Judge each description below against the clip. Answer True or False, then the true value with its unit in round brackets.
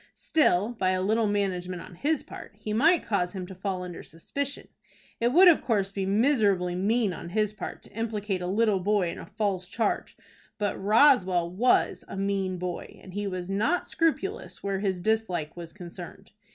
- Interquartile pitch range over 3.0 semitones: True (3.5 semitones)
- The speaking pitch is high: True (200 Hz)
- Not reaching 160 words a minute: False (185 wpm)